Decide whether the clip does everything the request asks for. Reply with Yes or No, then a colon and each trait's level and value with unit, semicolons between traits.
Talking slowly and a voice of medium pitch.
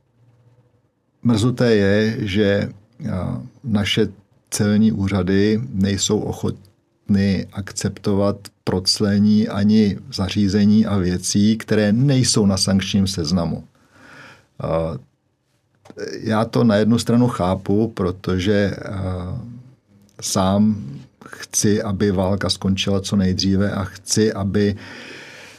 No: slow, 85 wpm; low, 105 Hz